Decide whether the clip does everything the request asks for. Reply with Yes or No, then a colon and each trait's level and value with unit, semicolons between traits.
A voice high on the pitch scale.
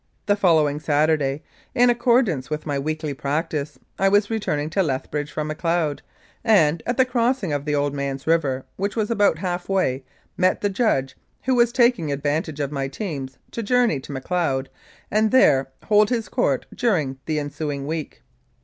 No: medium, 155 Hz